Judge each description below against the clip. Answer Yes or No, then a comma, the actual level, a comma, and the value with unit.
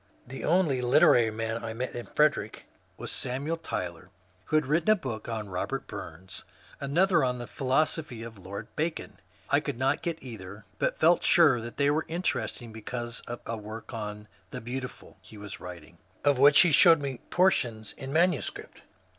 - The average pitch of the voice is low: Yes, low, 125 Hz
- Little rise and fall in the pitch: No, average, 5.3 semitones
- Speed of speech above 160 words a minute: Yes, average, 180 wpm